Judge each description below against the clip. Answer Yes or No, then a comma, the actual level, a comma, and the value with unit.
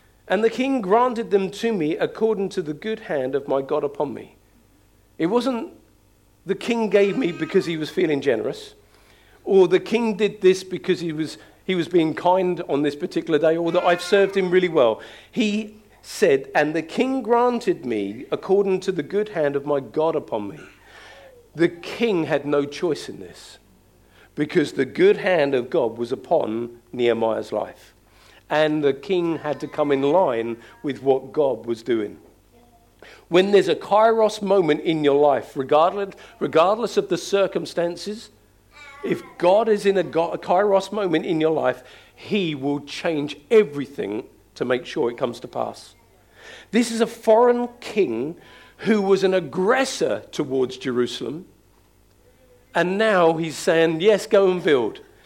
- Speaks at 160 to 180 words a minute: Yes, average, 165 wpm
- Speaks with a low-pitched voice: No, medium, 180 Hz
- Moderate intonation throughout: No, wide, 6.3 semitones